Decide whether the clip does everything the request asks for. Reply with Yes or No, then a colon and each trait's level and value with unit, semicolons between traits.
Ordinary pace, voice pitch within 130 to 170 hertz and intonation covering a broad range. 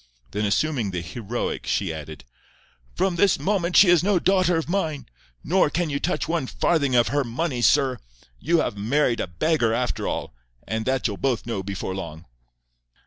Yes: average, 180 wpm; low, 135 Hz; wide, 8.2 semitones